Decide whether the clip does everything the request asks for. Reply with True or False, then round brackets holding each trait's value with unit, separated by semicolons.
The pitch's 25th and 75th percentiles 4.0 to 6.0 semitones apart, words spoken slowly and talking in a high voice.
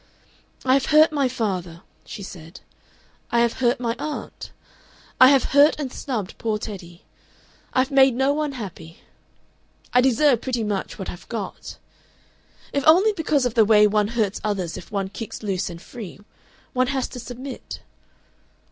False (4.9 semitones; 160 wpm; 235 Hz)